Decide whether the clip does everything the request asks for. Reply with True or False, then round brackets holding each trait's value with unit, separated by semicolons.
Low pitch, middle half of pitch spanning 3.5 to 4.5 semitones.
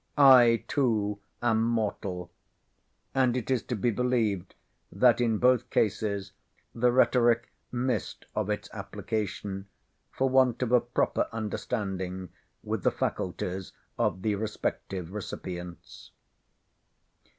True (110 Hz; 3.8 semitones)